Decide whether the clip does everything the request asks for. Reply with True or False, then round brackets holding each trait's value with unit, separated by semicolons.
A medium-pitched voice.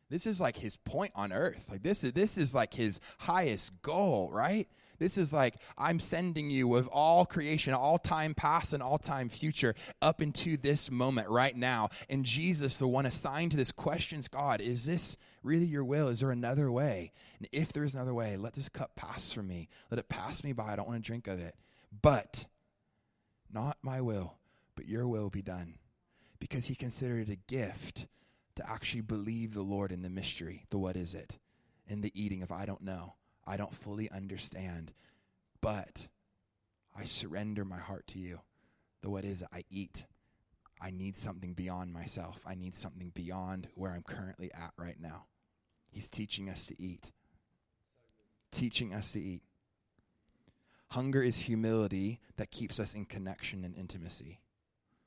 False (110 Hz)